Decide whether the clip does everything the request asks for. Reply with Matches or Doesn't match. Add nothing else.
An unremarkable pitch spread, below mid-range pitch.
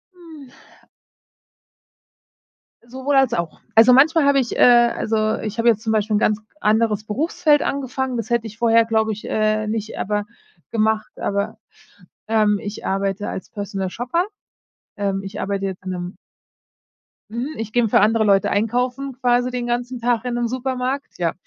Doesn't match